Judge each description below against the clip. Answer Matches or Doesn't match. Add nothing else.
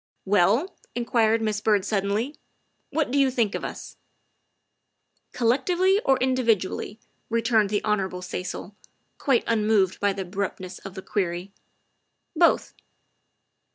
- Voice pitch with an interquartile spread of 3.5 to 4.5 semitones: Matches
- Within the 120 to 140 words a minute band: Matches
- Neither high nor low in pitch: Doesn't match